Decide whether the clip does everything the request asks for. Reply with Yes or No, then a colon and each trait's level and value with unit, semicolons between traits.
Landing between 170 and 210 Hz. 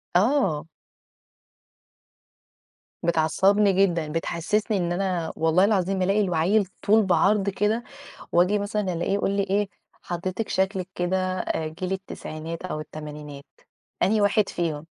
Yes: medium, 185 Hz